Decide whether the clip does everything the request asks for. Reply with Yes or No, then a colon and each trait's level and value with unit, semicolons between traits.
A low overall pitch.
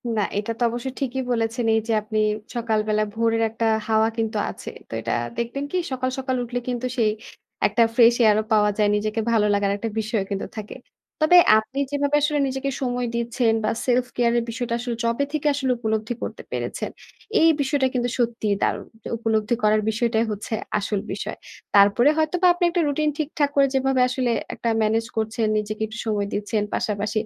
No: high, 230 Hz